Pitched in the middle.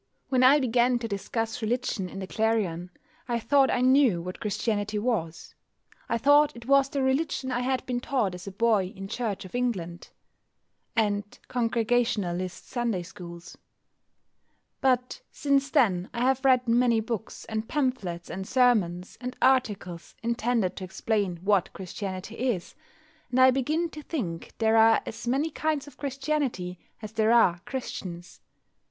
No: high, 230 Hz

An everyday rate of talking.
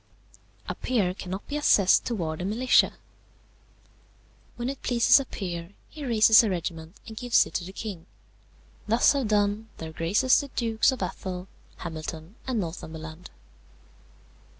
Yes: average, 145 wpm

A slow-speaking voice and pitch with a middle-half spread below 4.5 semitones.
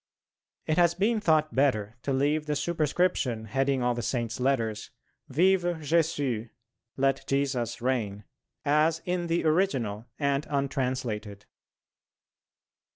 No: slow, 115 wpm; average, 4.8 semitones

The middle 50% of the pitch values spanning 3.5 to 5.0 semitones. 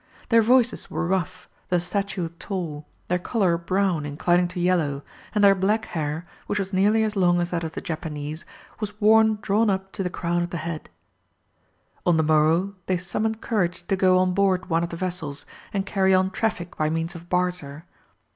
No: average, 2.8 semitones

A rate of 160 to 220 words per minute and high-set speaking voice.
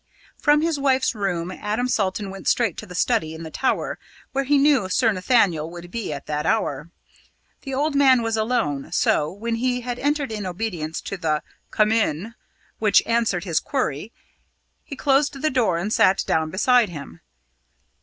Yes: average, 175 wpm; high, 215 Hz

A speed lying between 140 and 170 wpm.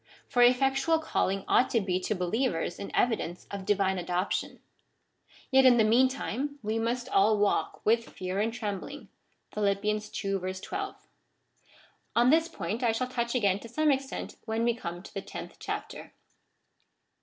Yes: average, 160 wpm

